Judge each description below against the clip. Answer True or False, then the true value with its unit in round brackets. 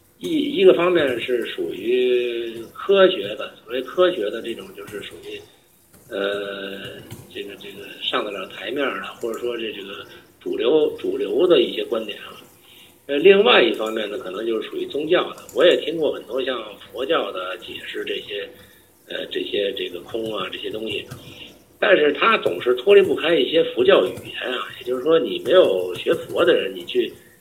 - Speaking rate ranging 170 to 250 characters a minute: False (260 characters per minute)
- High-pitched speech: True (390 Hz)